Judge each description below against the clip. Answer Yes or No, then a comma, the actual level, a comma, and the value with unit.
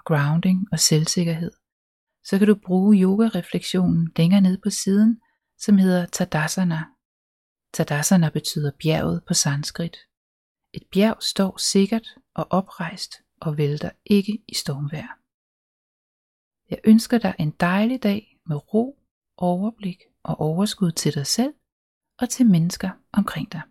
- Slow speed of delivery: Yes, slow, 125 wpm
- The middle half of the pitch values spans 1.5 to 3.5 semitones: No, average, 4.5 semitones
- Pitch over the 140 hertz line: Yes, medium, 185 Hz